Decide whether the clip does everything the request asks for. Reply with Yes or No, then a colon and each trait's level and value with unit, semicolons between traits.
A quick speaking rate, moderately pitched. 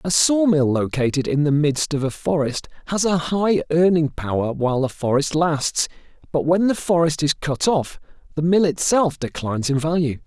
No: average, 180 wpm; medium, 155 Hz